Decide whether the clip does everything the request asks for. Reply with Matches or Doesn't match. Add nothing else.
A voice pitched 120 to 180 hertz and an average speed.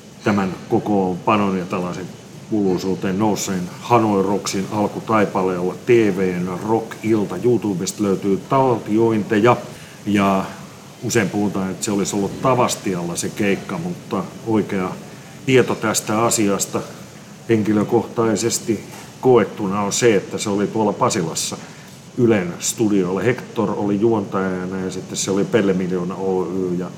Doesn't match